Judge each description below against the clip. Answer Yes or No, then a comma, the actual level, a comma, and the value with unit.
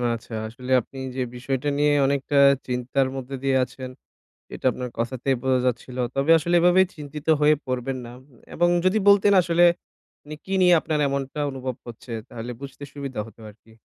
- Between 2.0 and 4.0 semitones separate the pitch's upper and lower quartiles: Yes, average, 2.9 semitones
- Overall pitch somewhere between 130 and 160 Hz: Yes, low, 135 Hz